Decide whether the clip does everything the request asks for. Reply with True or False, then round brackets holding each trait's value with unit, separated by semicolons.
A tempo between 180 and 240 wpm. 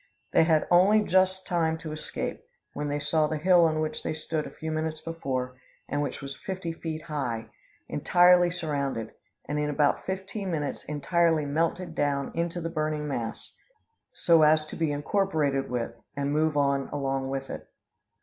False (170 wpm)